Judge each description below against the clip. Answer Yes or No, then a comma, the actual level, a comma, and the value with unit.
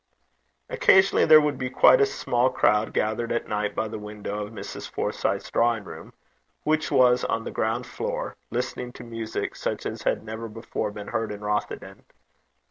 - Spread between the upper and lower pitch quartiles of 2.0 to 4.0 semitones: Yes, average, 2.9 semitones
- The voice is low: Yes, low, 115 Hz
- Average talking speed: Yes, average, 175 wpm